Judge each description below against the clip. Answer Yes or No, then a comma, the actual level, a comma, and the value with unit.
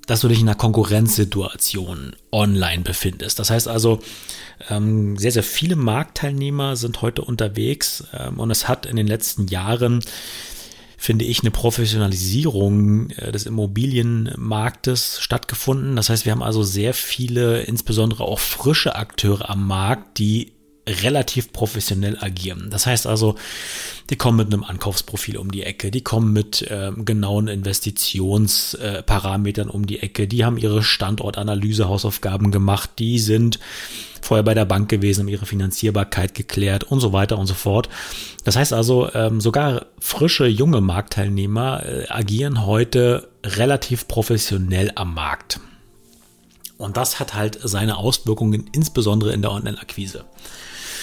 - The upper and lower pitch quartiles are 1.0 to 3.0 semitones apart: Yes, narrow, 2.6 semitones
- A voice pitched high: No, low, 110 Hz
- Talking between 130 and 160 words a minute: Yes, average, 140 wpm